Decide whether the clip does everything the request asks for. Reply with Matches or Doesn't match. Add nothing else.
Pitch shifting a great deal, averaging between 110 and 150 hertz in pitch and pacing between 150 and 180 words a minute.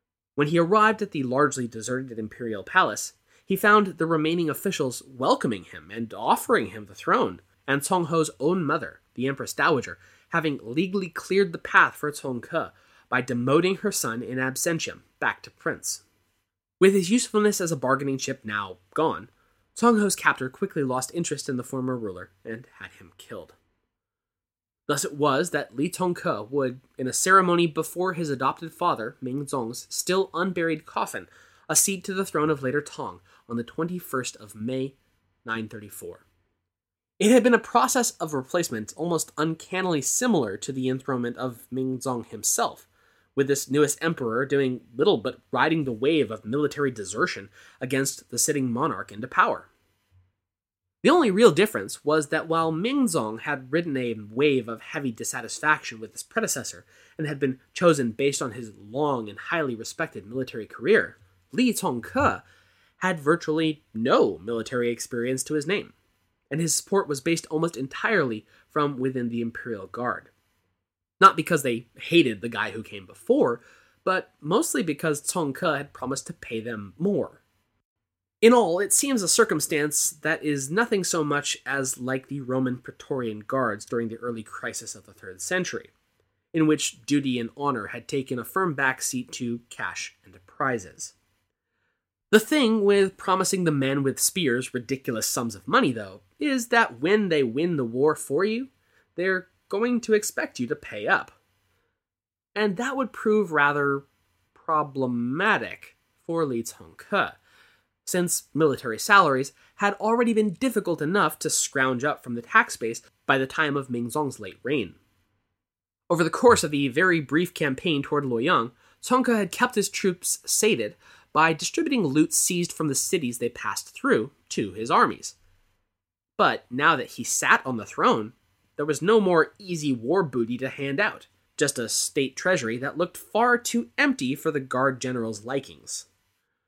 Matches